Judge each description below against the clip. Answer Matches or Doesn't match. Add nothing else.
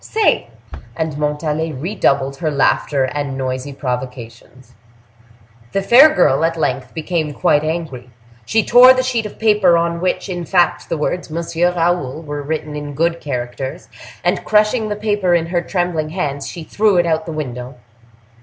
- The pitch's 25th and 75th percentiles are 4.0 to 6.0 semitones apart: Matches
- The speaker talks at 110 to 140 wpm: Doesn't match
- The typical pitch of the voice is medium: Matches